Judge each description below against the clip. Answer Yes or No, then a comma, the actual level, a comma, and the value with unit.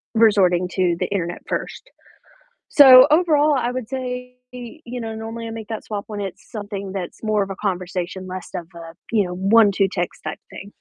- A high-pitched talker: Yes, high, 210 Hz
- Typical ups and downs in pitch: Yes, average, 4.7 semitones